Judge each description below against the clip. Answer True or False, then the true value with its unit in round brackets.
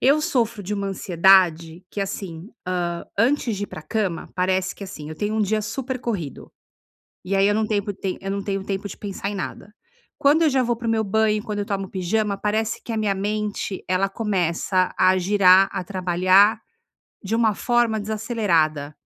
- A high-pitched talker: True (200 Hz)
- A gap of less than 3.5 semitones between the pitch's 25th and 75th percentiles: True (2.8 semitones)